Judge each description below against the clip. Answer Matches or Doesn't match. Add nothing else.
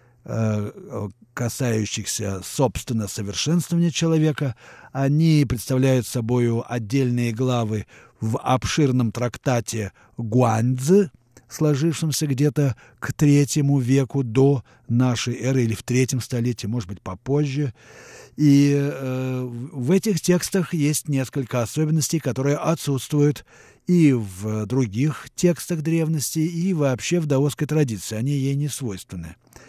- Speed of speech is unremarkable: Doesn't match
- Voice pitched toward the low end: Matches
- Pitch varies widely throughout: Doesn't match